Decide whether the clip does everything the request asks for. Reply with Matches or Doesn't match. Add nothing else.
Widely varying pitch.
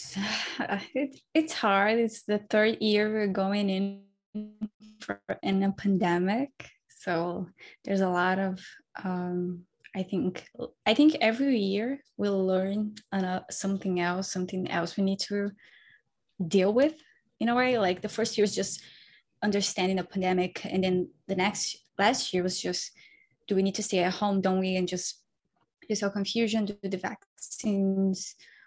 Doesn't match